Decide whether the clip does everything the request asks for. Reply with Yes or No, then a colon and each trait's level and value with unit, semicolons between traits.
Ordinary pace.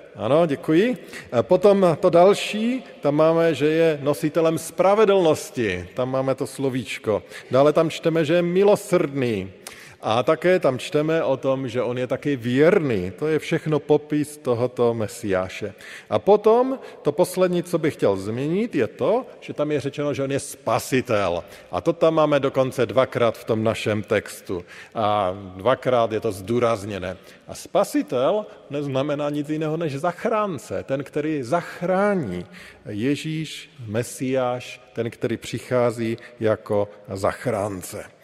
Yes: average, 140 wpm